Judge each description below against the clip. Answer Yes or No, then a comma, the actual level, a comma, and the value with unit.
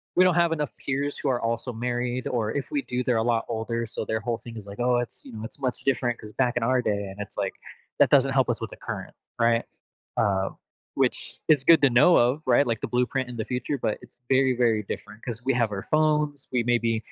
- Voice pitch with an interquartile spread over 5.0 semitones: No, average, 2.8 semitones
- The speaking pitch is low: Yes, low, 120 Hz